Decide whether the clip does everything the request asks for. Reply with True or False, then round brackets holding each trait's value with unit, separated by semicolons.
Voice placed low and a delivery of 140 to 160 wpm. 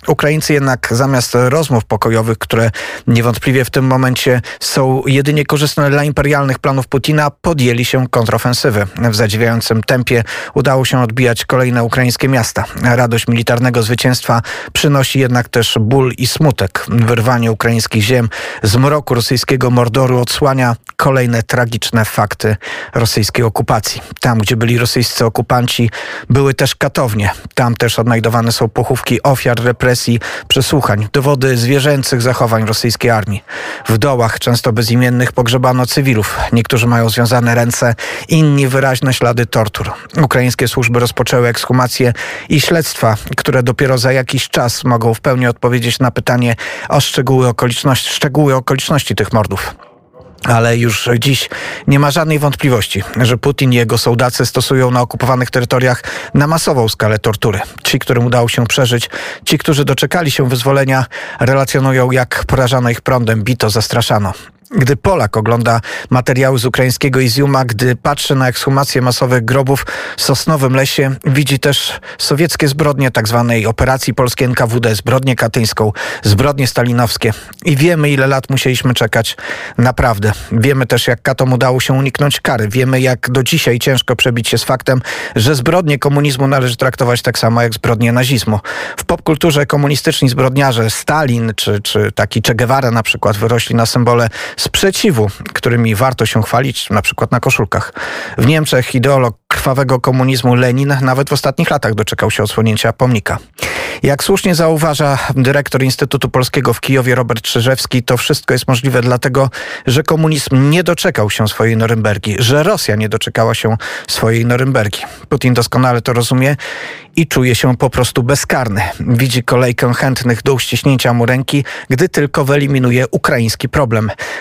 True (125 Hz; 145 wpm)